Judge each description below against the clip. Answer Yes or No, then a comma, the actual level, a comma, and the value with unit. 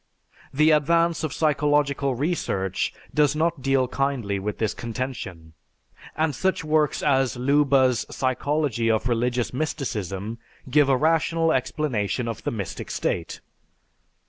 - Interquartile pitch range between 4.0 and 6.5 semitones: Yes, average, 4.6 semitones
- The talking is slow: Yes, slow, 120 wpm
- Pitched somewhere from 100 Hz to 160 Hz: Yes, low, 135 Hz